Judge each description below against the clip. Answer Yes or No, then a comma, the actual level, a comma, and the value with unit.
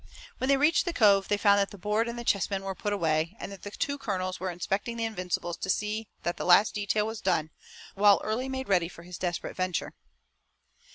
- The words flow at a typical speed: No, fast, 225 wpm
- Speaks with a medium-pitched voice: No, high, 200 Hz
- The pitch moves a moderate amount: Yes, average, 3.3 semitones